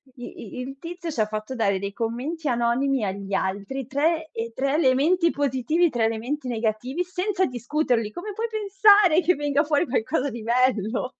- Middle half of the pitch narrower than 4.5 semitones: No, wide, 6.1 semitones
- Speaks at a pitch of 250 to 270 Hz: Yes, very high, 265 Hz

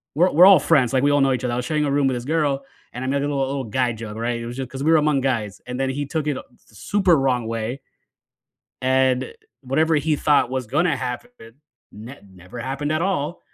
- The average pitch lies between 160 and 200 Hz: No, low, 135 Hz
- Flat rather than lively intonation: No, average, 3.3 semitones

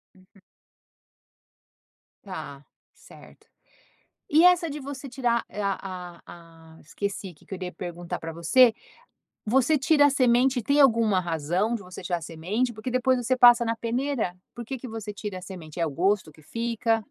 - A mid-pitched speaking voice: No, high, 220 Hz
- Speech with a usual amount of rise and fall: No, wide, 6.2 semitones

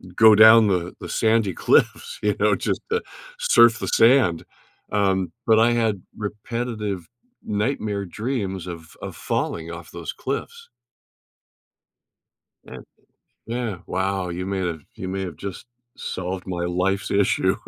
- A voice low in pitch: Yes, low, 100 Hz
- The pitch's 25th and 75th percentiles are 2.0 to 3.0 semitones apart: No, average, 3.8 semitones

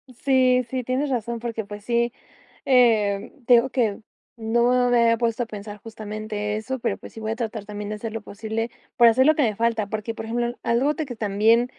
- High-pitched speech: Yes, high, 230 Hz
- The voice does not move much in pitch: Yes, narrow, 2.2 semitones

